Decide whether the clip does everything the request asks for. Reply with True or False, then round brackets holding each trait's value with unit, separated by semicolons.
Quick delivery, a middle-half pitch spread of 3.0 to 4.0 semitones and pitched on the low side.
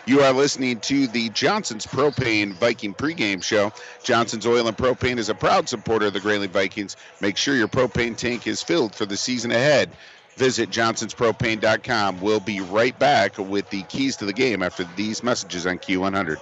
False (185 wpm; 3.7 semitones; 110 Hz)